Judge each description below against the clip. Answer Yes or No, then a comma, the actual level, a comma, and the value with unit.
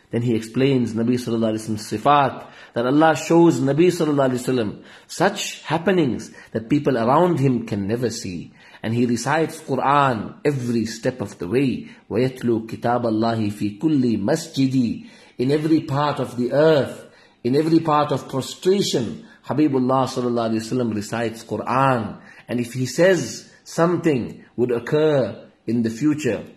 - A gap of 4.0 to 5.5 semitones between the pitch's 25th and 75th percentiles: Yes, average, 4.4 semitones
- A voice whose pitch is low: Yes, low, 130 Hz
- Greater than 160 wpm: No, average, 145 wpm